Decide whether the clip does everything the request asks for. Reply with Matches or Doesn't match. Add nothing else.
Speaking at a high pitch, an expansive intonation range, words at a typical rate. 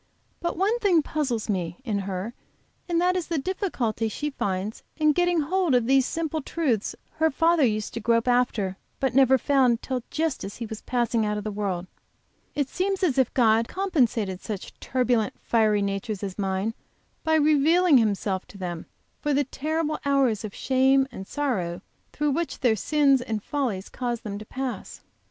Matches